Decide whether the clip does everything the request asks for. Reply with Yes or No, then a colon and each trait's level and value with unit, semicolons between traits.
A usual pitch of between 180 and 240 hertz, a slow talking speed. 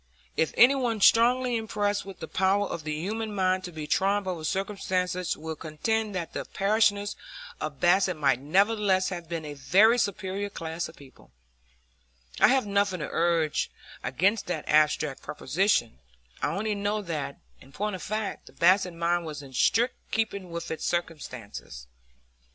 No: medium, 185 Hz; average, 160 wpm